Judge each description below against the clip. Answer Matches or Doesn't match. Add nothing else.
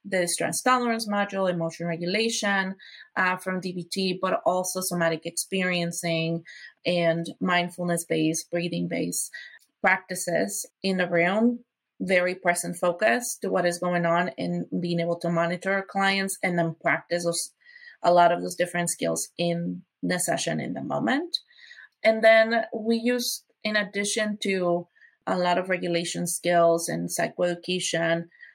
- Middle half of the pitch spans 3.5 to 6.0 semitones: Doesn't match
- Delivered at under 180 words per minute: Matches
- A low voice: Doesn't match